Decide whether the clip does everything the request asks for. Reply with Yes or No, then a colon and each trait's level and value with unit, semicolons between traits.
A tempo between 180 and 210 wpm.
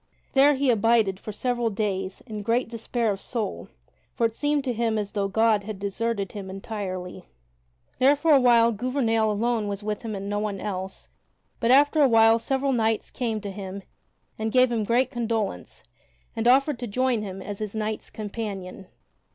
Yes: average, 185 wpm